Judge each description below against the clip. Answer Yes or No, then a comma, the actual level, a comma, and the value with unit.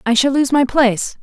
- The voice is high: Yes, very high, 260 Hz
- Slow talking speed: No, fast, 245 wpm